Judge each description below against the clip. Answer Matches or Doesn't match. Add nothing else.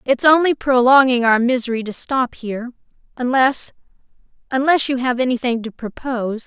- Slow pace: Matches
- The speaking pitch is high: Matches